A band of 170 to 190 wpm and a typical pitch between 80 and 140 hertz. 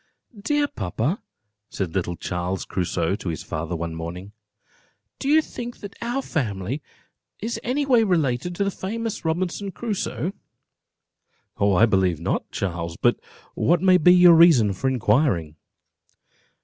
No: slow, 135 wpm; low, 135 Hz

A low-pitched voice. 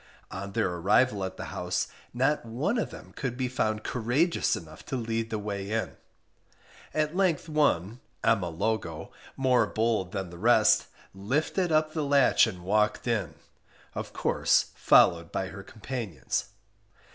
Yes: low, 110 Hz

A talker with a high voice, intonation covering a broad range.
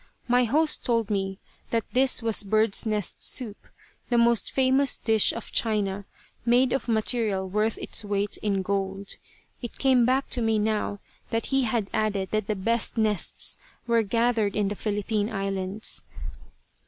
No: high, 220 Hz; average, 2.7 semitones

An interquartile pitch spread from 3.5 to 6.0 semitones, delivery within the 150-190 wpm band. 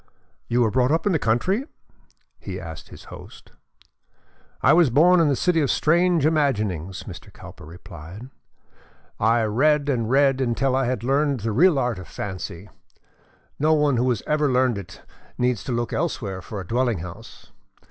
Yes: wide, 5.5 semitones; average, 170 wpm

